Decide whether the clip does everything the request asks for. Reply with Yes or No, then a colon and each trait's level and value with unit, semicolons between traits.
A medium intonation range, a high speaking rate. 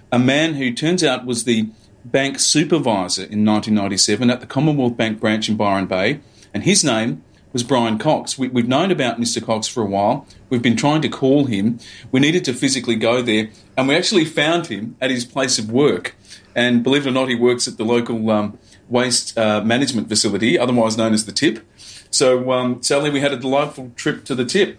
Yes: average, 3.2 semitones; fast, 210 wpm